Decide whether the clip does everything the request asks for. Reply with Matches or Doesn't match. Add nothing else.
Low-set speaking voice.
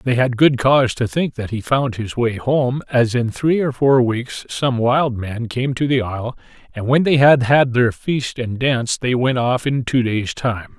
Matches